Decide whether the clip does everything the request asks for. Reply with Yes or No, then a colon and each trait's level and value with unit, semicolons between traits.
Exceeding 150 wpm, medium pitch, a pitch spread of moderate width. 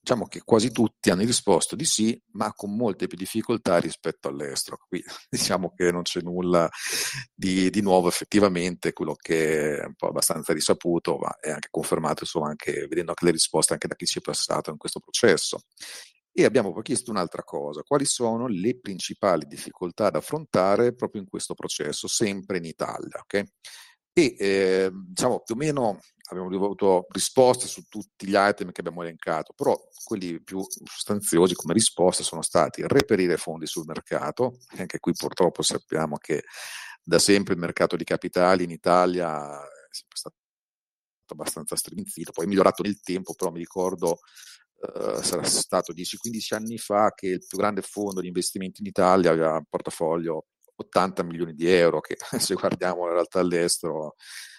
No: fast, 170 wpm; very low, 95 Hz; average, 3.2 semitones